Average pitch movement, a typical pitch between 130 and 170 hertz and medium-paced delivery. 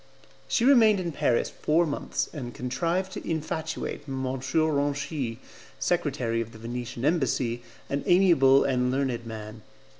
No: average, 4.7 semitones; medium, 140 Hz; slow, 130 wpm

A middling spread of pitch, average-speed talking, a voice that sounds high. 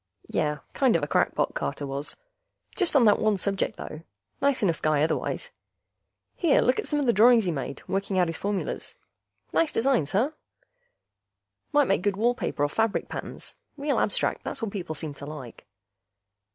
No: wide, 8.2 semitones; average, 180 wpm; high, 200 Hz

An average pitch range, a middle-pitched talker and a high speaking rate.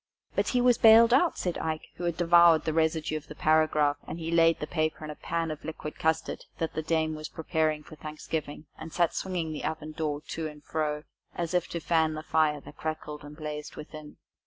No: narrow, 1.4 semitones; medium, 160 Hz; fast, 215 wpm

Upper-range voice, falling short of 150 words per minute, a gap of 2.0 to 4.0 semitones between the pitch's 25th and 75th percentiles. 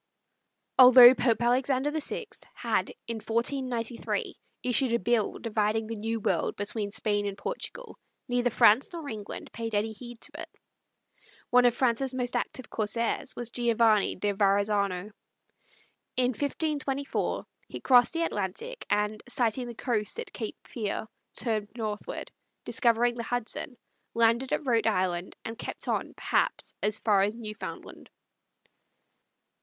Yes: high, 230 Hz; slow, 135 wpm; average, 3.0 semitones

